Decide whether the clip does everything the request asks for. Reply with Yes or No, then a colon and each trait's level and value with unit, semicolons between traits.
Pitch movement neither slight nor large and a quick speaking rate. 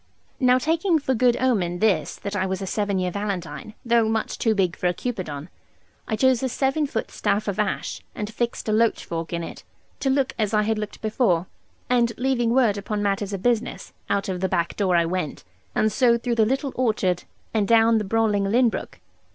Yes: average, 4.0 semitones; fast, 210 wpm